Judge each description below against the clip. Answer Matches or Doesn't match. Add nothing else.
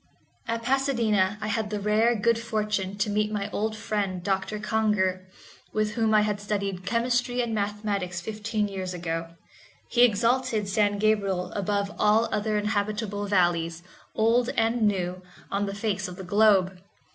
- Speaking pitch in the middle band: Doesn't match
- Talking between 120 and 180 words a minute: Matches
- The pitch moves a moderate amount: Doesn't match